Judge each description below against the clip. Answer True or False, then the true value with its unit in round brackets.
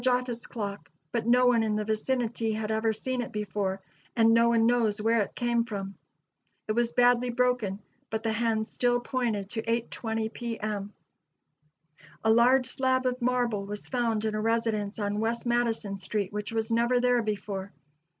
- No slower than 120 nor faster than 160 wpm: False (175 wpm)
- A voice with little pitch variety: True (2.2 semitones)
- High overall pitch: True (225 Hz)